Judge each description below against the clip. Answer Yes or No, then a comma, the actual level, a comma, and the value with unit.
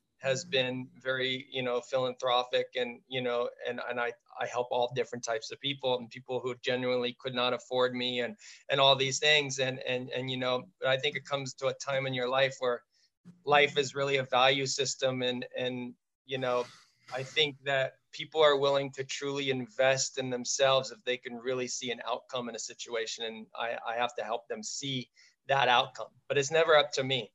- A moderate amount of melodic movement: No, narrow, 1.7 semitones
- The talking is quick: Yes, fast, 210 wpm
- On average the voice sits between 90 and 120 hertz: No, low, 130 Hz